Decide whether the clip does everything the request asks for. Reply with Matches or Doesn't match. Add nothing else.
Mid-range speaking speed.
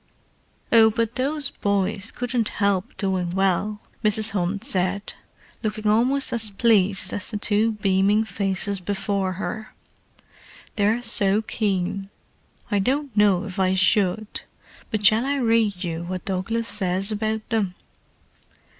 Doesn't match